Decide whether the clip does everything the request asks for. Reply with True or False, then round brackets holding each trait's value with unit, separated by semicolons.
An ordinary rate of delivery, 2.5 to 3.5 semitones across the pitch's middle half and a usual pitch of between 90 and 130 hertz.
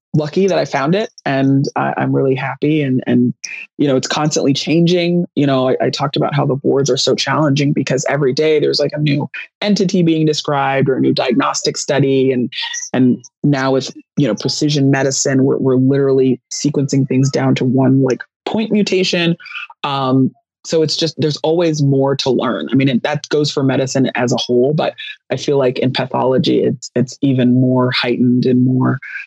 False (195 wpm; 2.9 semitones; 140 Hz)